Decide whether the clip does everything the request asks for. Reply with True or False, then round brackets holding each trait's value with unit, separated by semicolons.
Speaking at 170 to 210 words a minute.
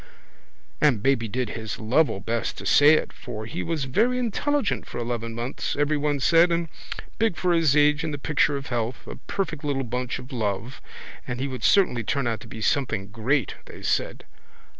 True (190 wpm)